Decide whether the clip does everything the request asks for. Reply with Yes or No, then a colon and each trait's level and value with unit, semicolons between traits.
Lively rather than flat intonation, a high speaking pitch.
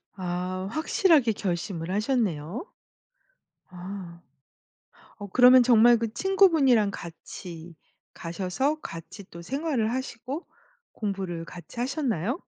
Yes: wide, 6.4 semitones; high, 210 Hz